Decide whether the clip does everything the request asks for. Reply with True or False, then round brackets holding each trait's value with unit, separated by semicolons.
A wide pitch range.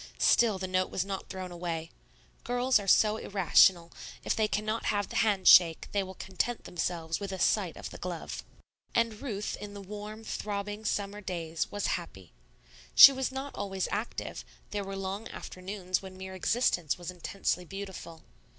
False (2.5 semitones)